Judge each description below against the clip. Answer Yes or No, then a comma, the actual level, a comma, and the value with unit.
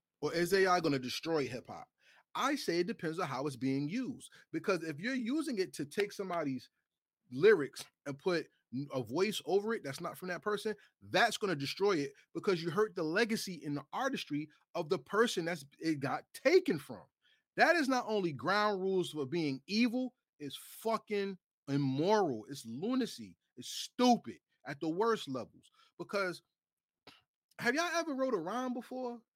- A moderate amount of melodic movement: No, wide, 7.4 semitones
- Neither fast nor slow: Yes, average, 175 wpm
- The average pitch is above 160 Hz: Yes, high, 190 Hz